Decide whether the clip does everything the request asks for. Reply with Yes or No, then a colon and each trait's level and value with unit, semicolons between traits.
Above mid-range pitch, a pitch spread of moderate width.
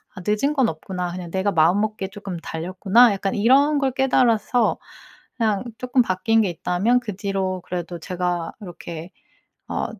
Yes: high, 195 Hz; average, 4.4 semitones